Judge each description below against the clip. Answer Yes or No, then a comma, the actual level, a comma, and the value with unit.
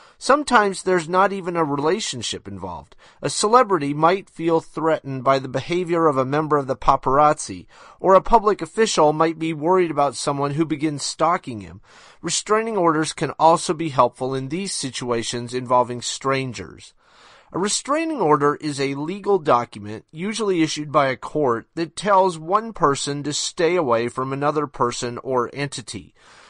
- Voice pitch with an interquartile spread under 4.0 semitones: No, average, 5.2 semitones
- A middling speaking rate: Yes, average, 155 wpm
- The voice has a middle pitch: Yes, medium, 150 Hz